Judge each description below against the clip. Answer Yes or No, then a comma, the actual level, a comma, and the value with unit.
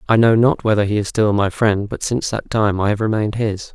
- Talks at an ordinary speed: No, fast, 270 wpm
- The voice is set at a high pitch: No, low, 110 Hz